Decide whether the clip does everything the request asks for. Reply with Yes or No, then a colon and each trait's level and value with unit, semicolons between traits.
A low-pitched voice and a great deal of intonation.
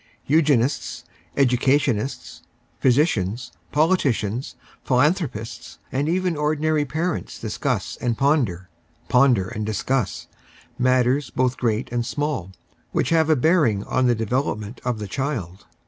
No: low, 130 Hz; average, 4.7 semitones